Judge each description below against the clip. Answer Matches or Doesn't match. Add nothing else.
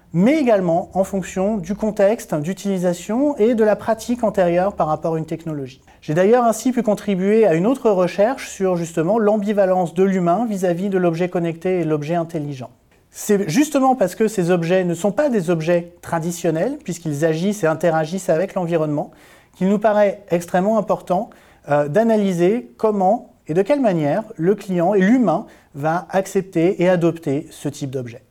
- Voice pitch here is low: Doesn't match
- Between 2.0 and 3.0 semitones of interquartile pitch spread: Doesn't match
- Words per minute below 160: Doesn't match